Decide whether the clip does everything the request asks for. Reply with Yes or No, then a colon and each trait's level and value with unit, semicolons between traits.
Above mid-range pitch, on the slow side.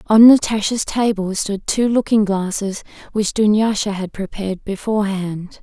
Yes: high, 205 Hz; slow, 130 wpm